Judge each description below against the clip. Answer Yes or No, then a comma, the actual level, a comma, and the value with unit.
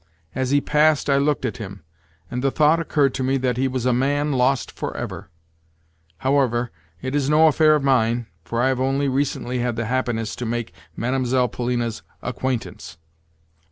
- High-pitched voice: No, low, 130 Hz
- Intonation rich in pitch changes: No, narrow, 2.4 semitones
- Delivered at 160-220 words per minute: Yes, average, 180 wpm